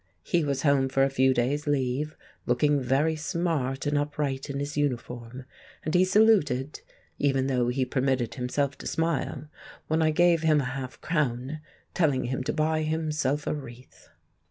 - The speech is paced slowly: No, average, 165 wpm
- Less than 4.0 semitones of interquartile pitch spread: Yes, average, 2.9 semitones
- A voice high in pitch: No, medium, 140 Hz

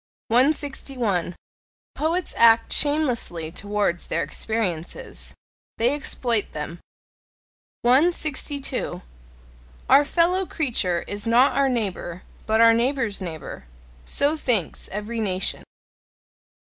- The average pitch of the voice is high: Yes, high, 230 Hz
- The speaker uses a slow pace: Yes, slow, 95 wpm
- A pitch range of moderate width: No, wide, 6.3 semitones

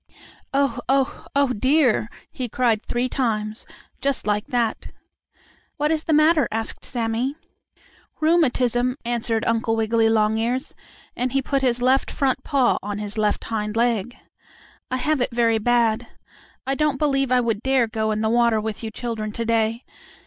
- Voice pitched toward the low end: No, high, 240 Hz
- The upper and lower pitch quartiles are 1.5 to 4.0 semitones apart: Yes, average, 3.2 semitones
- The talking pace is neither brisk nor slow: Yes, average, 160 wpm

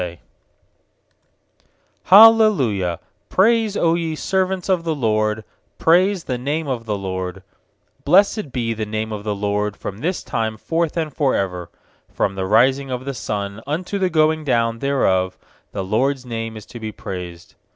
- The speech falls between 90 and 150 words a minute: No, average, 160 wpm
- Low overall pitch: Yes, low, 125 Hz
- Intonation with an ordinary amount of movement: No, wide, 7.7 semitones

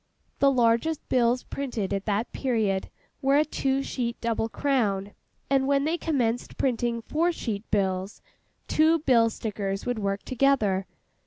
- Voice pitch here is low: No, high, 235 Hz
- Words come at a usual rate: Yes, average, 145 wpm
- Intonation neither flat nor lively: Yes, average, 4.9 semitones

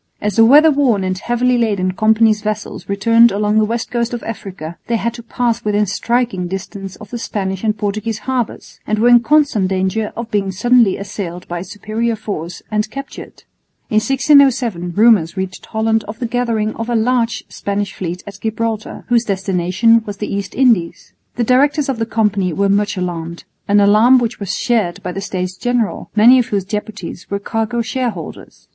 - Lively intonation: No, average, 3.2 semitones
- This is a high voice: Yes, high, 215 Hz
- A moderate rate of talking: Yes, average, 185 wpm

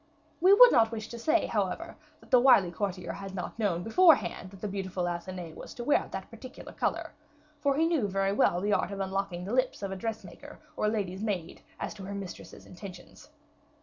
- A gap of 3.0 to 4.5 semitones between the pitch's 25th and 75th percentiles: Yes, average, 3.7 semitones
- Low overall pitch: No, high, 200 Hz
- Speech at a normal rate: No, fast, 215 wpm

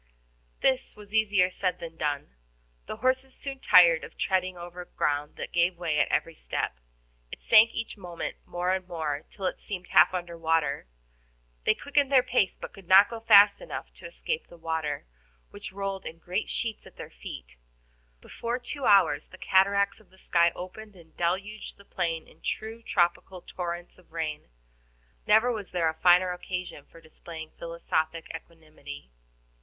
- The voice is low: No, medium, 180 Hz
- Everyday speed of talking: Yes, average, 170 wpm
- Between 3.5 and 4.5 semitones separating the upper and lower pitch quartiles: Yes, average, 4.0 semitones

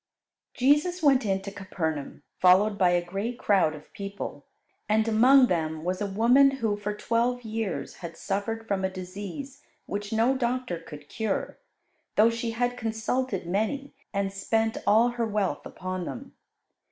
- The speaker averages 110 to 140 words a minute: No, average, 155 wpm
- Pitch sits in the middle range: No, high, 210 Hz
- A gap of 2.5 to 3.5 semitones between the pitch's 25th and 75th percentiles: No, average, 4.1 semitones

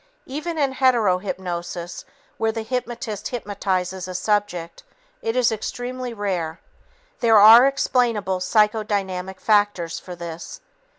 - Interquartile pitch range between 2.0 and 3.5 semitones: No, average, 4.6 semitones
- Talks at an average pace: No, slow, 115 wpm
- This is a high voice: Yes, high, 210 Hz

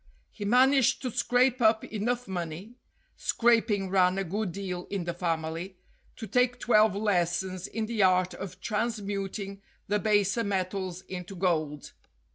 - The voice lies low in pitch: No, high, 200 Hz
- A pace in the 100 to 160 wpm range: Yes, average, 140 wpm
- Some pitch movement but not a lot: Yes, average, 3.4 semitones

